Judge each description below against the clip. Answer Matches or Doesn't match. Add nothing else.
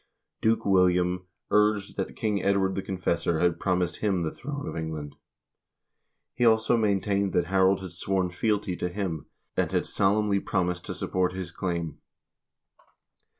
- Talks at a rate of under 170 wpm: Matches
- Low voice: Matches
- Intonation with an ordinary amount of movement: Doesn't match